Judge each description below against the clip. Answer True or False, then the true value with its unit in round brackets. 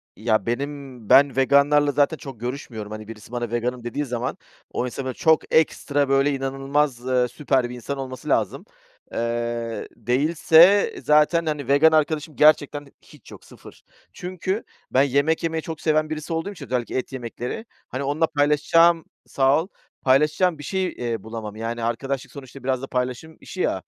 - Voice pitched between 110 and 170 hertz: True (140 Hz)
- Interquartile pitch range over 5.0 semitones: False (3.7 semitones)